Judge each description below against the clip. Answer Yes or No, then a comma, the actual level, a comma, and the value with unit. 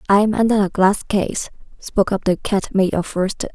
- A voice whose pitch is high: Yes, high, 200 Hz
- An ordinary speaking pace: No, fast, 220 wpm